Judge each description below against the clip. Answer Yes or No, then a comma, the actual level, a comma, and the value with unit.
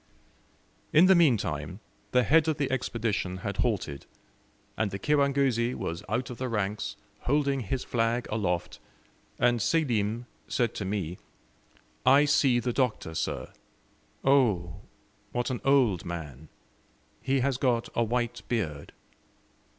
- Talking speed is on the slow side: Yes, slow, 130 wpm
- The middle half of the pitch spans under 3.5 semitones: No, average, 5.3 semitones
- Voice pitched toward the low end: Yes, low, 120 Hz